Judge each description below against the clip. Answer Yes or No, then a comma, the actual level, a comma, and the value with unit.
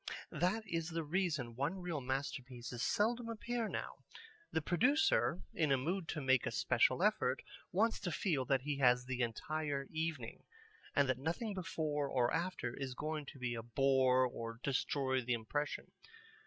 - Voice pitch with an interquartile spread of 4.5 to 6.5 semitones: Yes, average, 5.1 semitones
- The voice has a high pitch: No, medium, 145 Hz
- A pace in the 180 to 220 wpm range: No, average, 165 wpm